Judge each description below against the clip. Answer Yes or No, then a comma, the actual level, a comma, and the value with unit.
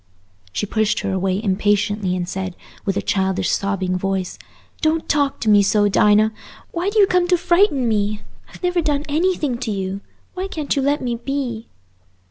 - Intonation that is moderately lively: No, wide, 7.4 semitones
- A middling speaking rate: Yes, average, 180 wpm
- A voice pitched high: Yes, high, 220 Hz